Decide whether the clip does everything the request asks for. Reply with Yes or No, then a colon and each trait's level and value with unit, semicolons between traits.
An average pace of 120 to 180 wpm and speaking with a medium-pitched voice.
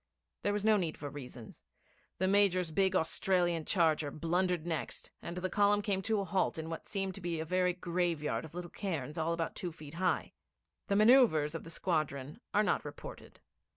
No: average, 190 wpm; medium, 175 Hz